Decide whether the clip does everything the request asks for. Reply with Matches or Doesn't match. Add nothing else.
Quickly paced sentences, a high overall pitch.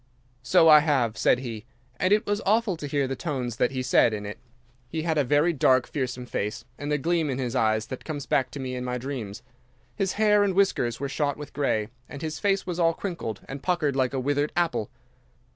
Doesn't match